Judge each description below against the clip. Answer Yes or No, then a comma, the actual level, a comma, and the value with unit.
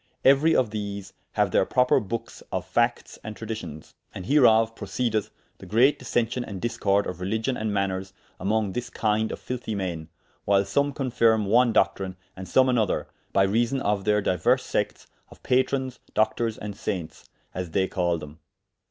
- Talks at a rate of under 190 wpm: Yes, average, 165 wpm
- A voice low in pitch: Yes, low, 110 Hz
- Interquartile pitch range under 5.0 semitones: Yes, average, 3.7 semitones